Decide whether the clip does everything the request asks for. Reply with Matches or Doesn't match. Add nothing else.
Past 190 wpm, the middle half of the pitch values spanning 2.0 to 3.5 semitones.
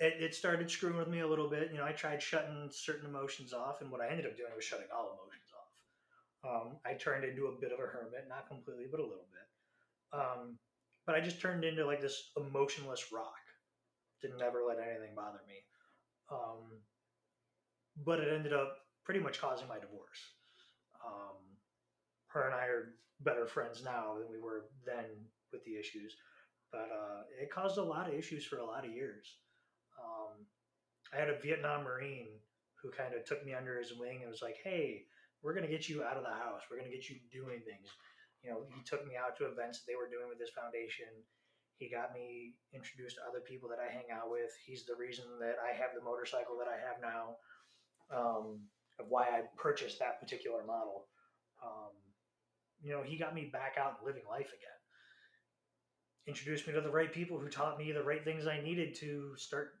Doesn't match